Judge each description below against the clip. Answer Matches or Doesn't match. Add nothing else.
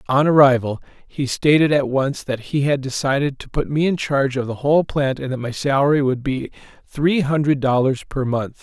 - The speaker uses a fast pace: Matches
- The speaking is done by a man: Matches